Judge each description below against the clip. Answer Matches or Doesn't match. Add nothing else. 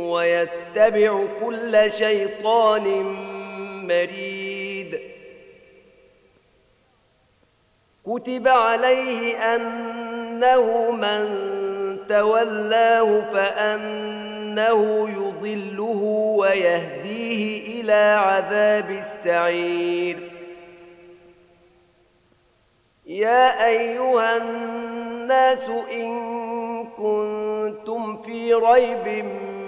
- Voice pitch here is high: Matches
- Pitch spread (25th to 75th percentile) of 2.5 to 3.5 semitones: Matches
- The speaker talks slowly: Matches